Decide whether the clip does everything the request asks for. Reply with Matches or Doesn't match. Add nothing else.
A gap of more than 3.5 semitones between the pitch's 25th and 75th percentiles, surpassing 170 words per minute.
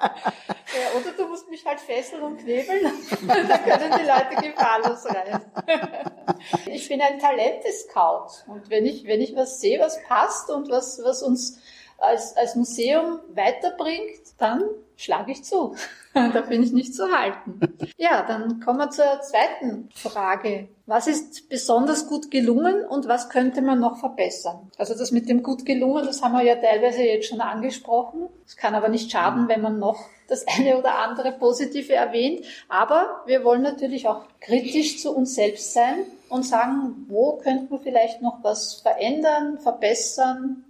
Doesn't match